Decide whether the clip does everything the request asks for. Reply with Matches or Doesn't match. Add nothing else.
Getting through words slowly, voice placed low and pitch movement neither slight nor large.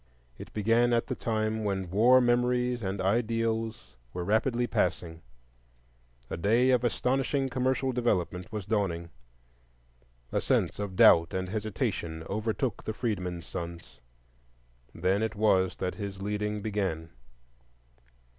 Matches